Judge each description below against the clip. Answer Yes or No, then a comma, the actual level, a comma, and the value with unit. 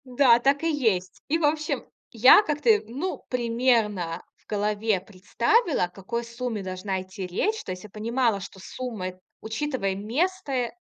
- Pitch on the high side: Yes, high, 230 Hz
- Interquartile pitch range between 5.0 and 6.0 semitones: Yes, wide, 5.6 semitones